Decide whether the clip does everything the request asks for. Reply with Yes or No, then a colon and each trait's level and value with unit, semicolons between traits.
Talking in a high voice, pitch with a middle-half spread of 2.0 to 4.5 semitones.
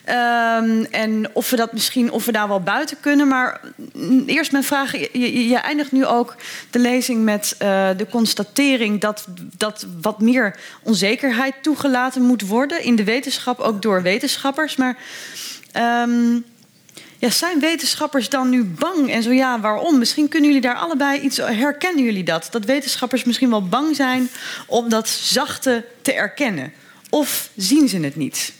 Yes: high, 245 Hz; average, 3.8 semitones